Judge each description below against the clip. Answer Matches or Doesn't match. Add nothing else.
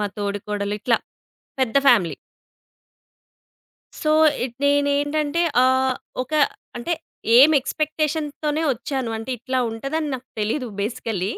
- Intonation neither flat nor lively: Matches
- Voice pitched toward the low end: Doesn't match